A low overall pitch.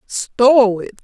No: high, 235 Hz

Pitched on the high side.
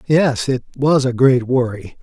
No: low, 130 Hz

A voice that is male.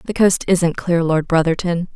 No: female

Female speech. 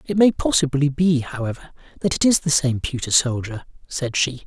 No: male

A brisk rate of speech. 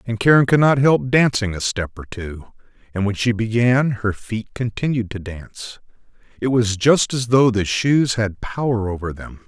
No: average, 190 wpm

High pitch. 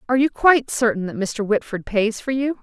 Yes: high, 235 Hz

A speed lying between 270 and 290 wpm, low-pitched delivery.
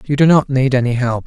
Yes: fast, 285 wpm; low, 130 Hz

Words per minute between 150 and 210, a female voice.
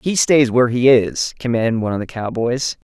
No: fast, 205 wpm; male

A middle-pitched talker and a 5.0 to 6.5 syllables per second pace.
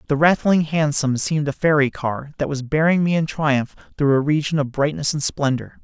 Yes: medium, 145 Hz; 5.2 syllables/s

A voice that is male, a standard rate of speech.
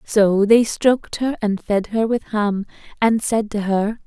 No: female; average, 190 wpm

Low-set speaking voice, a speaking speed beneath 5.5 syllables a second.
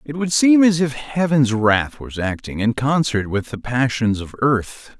Yes: low, 130 Hz; 4.1 syllables/s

